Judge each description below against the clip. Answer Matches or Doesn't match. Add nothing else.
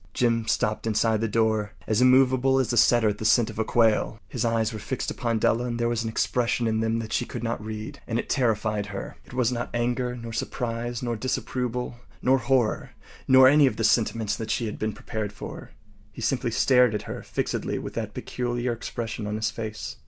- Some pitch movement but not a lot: Doesn't match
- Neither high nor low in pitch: Doesn't match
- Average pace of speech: Doesn't match